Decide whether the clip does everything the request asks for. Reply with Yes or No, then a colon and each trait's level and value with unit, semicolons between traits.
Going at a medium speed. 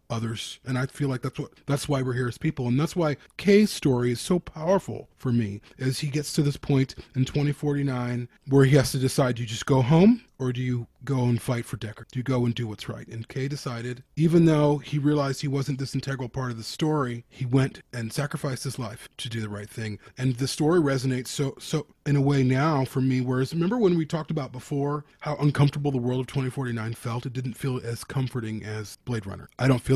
No: fast, 245 wpm